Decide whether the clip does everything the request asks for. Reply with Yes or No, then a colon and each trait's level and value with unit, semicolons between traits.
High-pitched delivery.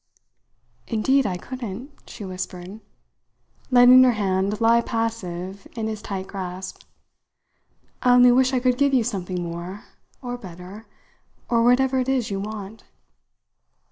Yes: high, 220 Hz